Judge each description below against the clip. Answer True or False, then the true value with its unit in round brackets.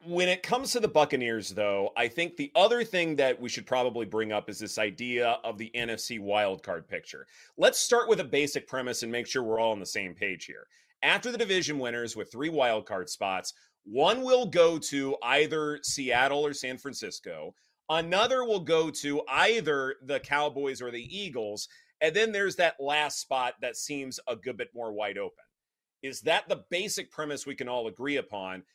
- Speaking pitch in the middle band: True (145 Hz)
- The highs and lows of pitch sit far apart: True (7.3 semitones)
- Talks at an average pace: True (195 wpm)